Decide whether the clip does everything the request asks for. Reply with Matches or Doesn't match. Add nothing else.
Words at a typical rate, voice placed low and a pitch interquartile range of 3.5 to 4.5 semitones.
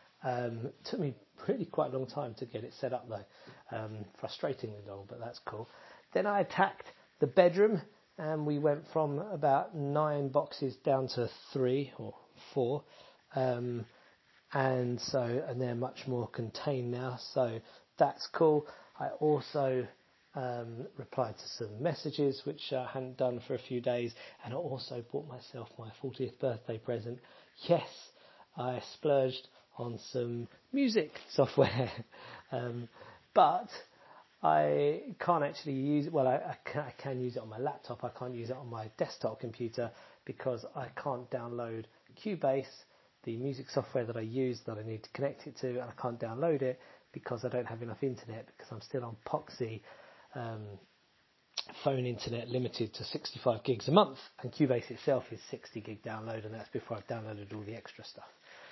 Doesn't match